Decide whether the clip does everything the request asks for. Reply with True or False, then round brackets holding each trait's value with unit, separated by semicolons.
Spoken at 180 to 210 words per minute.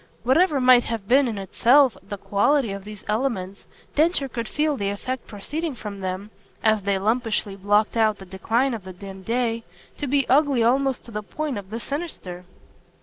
True (185 wpm)